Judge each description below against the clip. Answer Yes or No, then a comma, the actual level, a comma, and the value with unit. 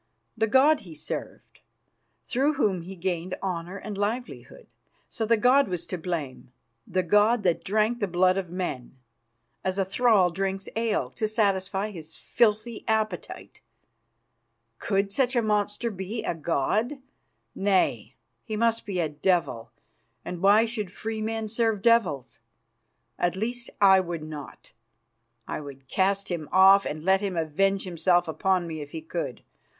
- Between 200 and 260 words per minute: No, average, 150 wpm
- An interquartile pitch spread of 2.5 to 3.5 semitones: No, average, 3.9 semitones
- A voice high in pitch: Yes, high, 195 Hz